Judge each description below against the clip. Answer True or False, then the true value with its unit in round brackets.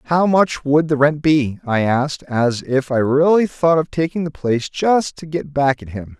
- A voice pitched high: False (145 Hz)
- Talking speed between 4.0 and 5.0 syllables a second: True (4.6 syllables/s)